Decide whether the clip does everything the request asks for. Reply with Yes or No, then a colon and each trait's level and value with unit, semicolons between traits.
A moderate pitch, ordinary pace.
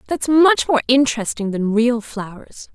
No: high, 245 Hz; average, 155 wpm